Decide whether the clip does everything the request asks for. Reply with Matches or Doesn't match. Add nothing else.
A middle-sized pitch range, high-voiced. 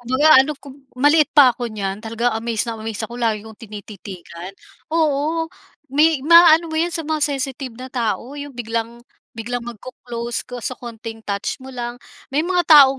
Matches